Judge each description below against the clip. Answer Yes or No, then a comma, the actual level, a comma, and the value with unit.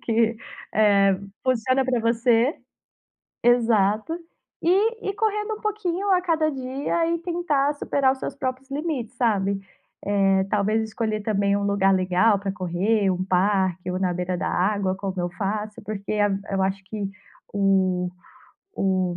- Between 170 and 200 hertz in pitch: No, high, 215 Hz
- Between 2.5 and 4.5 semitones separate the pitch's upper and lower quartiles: No, wide, 5.4 semitones